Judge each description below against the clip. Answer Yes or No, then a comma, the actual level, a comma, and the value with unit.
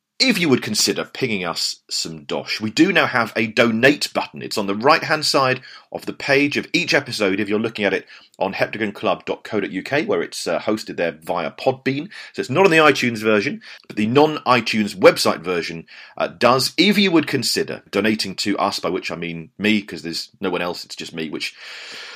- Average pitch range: No, wide, 5.9 semitones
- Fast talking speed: Yes, fast, 210 wpm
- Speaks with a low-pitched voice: Yes, low, 125 Hz